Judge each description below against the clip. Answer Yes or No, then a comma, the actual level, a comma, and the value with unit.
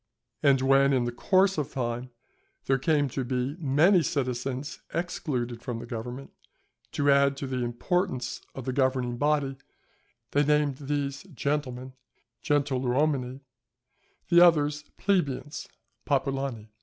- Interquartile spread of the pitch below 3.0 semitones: Yes, narrow, 2.6 semitones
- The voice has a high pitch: No, low, 135 Hz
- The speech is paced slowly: Yes, slow, 120 wpm